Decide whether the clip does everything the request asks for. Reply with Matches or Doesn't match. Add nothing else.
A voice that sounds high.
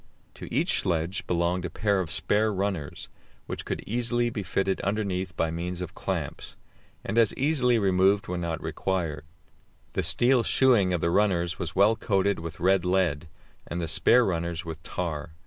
Doesn't match